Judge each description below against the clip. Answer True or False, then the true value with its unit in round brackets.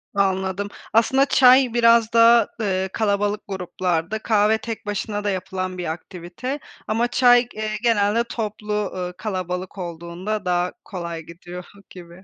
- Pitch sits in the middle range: False (205 Hz)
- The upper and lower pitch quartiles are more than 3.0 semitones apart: True (3.8 semitones)